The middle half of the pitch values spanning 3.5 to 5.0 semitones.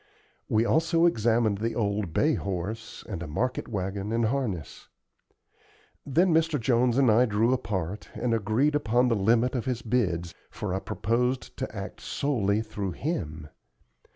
Yes: average, 3.9 semitones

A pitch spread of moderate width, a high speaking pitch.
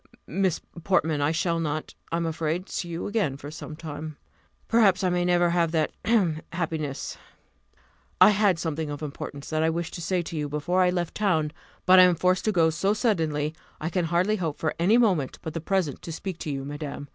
No: average, 3.0 semitones; medium, 165 Hz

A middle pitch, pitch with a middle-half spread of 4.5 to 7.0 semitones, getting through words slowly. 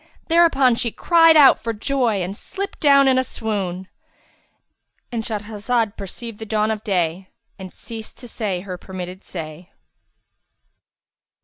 No: high, 220 Hz; average, 5.3 semitones; slow, 130 wpm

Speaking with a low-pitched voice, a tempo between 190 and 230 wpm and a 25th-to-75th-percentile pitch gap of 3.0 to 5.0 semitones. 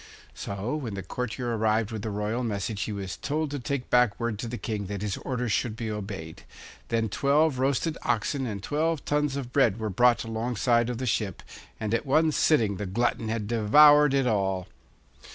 Yes: low, 115 Hz; average, 195 wpm; average, 4.2 semitones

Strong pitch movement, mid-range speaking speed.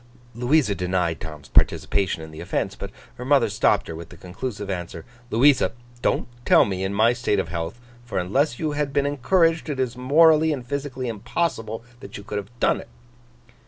Yes: wide, 6.9 semitones; average, 190 wpm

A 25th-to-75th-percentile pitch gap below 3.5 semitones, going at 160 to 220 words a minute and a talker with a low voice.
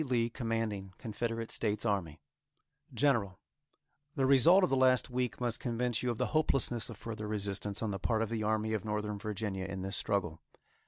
Yes: average, 3.0 semitones; average, 180 wpm; low, 110 Hz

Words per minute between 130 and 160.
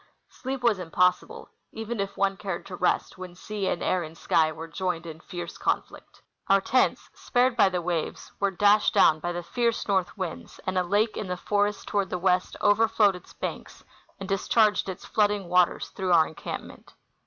No: average, 190 wpm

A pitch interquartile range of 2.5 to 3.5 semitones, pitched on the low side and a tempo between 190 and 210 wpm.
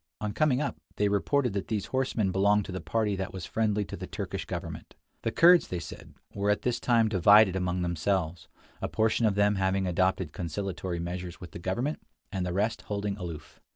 Yes: average, 3.1 semitones; low, 100 Hz; average, 200 wpm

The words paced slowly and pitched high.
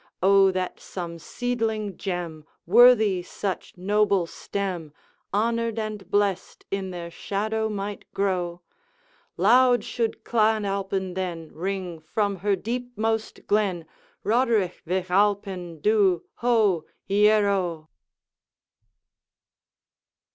Yes: slow, 95 wpm; high, 200 Hz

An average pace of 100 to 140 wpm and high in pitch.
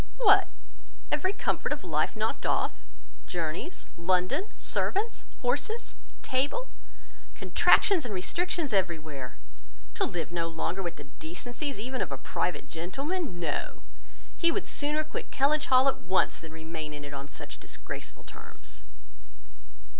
Yes: slow, 135 wpm; high, 195 Hz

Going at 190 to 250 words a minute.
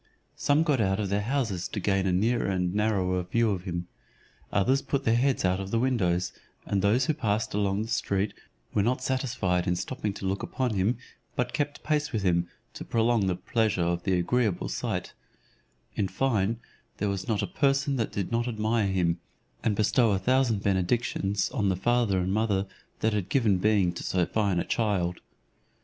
Yes: average, 195 wpm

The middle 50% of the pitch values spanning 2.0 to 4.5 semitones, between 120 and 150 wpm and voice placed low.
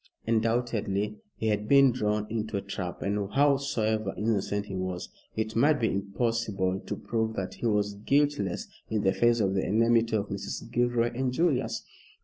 No: average, 2.8 semitones; average, 165 wpm; low, 110 Hz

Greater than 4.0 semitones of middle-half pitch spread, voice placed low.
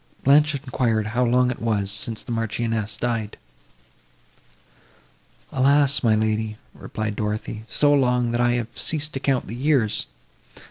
No: average, 3.3 semitones; low, 120 Hz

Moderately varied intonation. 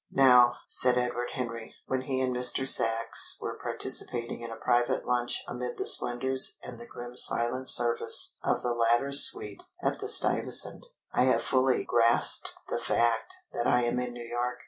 No: narrow, 1.1 semitones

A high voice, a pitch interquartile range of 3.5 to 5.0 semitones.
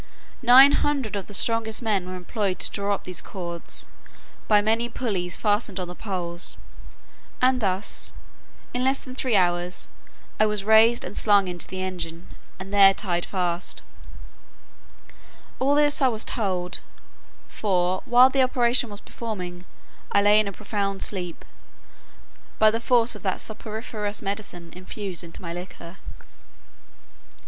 Yes: high, 205 Hz; average, 3.9 semitones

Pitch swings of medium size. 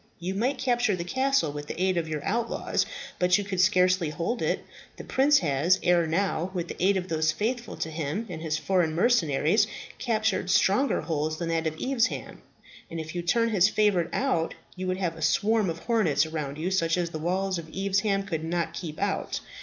Yes: average, 4.1 semitones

